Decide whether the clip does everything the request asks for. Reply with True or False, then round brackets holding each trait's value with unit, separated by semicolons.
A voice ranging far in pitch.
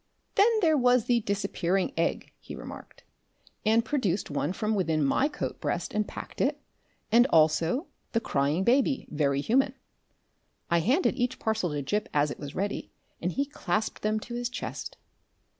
True (7.1 semitones)